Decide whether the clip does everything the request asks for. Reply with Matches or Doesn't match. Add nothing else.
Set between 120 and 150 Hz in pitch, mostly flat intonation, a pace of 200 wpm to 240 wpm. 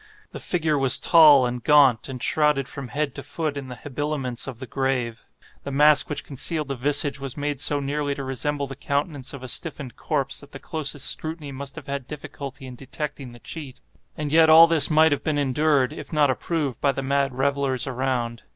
Matches